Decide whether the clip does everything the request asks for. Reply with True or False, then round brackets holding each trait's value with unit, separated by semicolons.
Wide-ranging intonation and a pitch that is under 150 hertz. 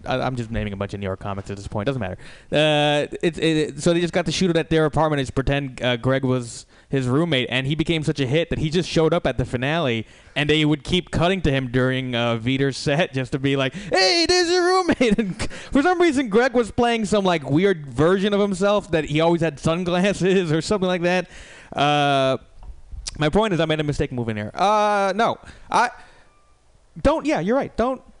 False (6.3 semitones; 155 Hz)